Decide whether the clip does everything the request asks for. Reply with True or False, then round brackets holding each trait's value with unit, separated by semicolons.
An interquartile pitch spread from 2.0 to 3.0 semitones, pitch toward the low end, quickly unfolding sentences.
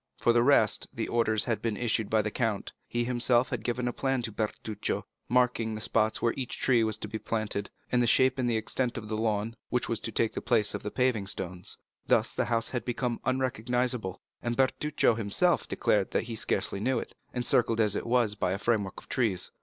True (2.4 semitones; 115 Hz; 215 wpm)